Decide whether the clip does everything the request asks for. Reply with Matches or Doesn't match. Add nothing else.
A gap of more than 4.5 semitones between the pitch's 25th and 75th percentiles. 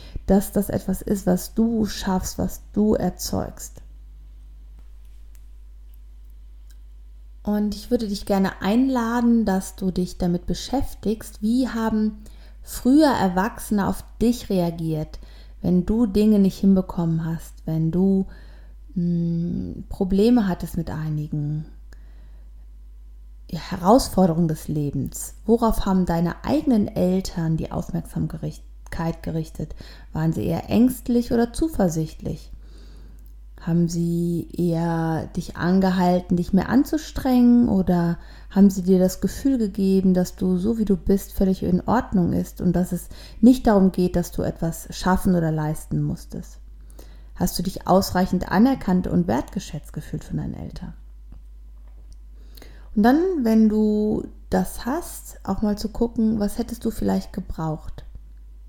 Matches